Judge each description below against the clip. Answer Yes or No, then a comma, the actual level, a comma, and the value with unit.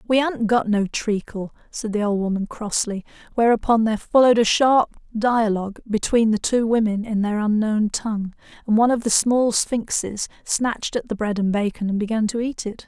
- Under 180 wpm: No, average, 190 wpm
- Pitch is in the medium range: No, high, 220 Hz